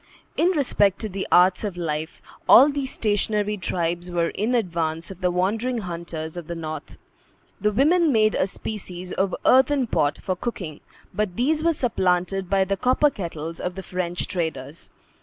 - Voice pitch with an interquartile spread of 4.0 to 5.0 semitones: Yes, average, 4.6 semitones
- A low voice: No, high, 190 Hz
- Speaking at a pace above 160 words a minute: Yes, average, 170 wpm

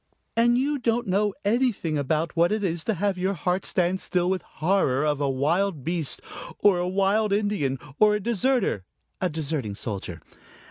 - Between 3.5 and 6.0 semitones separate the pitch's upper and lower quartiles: Yes, average, 5.1 semitones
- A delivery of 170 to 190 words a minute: Yes, average, 175 wpm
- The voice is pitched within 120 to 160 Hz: No, medium, 185 Hz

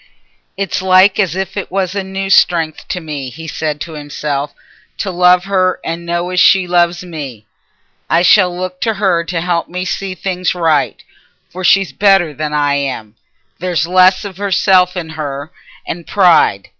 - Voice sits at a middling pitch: Yes, medium, 180 Hz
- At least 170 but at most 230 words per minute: Yes, average, 175 wpm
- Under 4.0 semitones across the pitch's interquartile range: Yes, average, 2.8 semitones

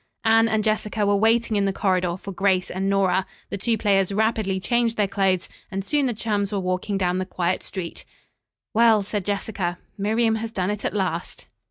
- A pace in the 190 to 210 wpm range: Yes, average, 195 wpm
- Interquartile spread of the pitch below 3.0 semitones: Yes, narrow, 2.6 semitones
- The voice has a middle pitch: No, high, 200 Hz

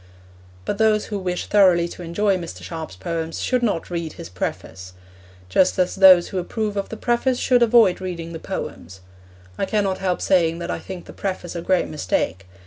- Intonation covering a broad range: No, average, 3.5 semitones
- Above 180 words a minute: Yes, average, 190 wpm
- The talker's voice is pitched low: No, medium, 180 Hz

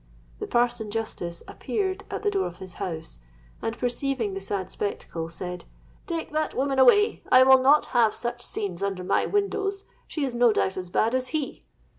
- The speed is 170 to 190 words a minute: Yes, average, 185 wpm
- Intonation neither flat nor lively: No, wide, 6.7 semitones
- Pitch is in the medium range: No, high, 240 Hz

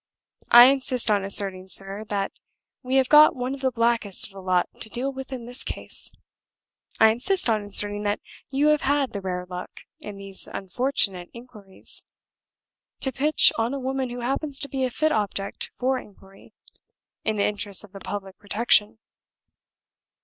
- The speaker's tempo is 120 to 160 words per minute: No, average, 170 wpm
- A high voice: Yes, high, 225 Hz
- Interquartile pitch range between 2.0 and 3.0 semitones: No, average, 4.9 semitones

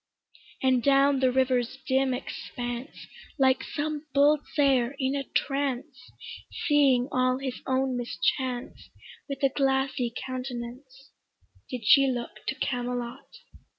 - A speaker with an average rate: No, slow, 120 wpm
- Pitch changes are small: Yes, narrow, 1.7 semitones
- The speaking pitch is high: Yes, very high, 260 Hz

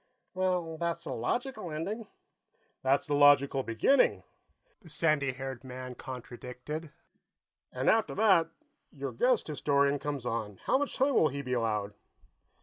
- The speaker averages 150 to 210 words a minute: No, average, 140 wpm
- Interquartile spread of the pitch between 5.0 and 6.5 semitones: Yes, average, 5.3 semitones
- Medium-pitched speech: Yes, medium, 145 Hz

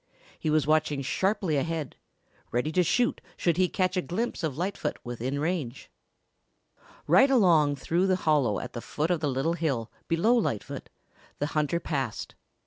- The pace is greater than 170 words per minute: No, average, 160 wpm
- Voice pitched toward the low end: No, medium, 155 Hz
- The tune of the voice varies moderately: Yes, average, 4.5 semitones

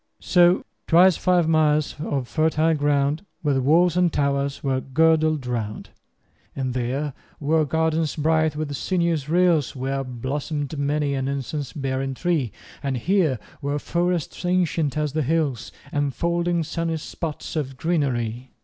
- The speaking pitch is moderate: Yes, medium, 150 Hz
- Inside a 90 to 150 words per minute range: Yes, average, 140 wpm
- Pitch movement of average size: Yes, average, 3.1 semitones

